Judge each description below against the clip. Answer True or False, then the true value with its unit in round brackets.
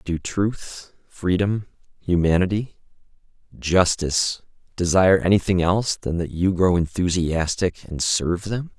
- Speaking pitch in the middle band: False (90 Hz)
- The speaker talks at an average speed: False (110 wpm)